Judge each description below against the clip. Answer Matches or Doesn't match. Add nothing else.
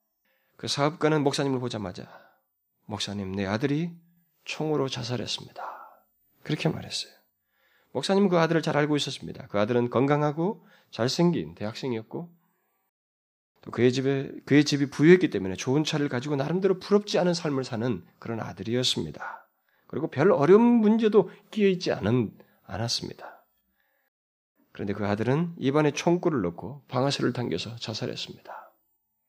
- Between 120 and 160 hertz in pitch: Matches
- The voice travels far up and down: Matches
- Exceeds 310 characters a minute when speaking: Matches